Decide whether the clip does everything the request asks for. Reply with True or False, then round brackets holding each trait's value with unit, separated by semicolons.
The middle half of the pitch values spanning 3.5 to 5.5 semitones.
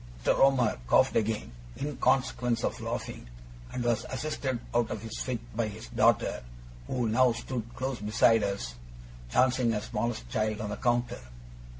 False (2.8 semitones)